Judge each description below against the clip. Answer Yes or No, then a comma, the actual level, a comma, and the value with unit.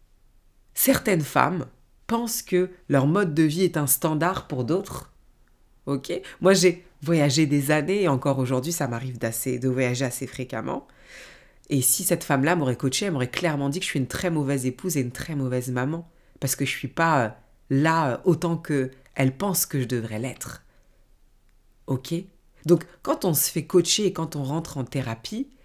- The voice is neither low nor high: Yes, medium, 145 Hz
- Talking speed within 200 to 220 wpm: No, average, 180 wpm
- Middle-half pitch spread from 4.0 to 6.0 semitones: Yes, average, 5.0 semitones